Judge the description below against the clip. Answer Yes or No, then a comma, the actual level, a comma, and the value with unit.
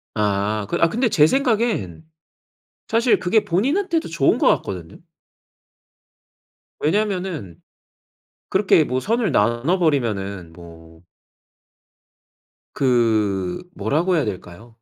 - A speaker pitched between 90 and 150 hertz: Yes, low, 135 Hz